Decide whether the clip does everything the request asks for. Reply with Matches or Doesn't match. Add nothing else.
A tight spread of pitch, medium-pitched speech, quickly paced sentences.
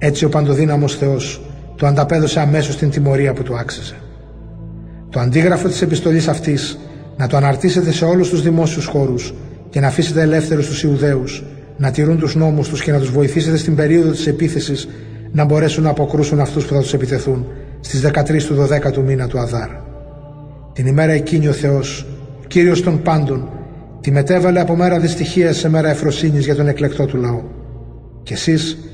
Matches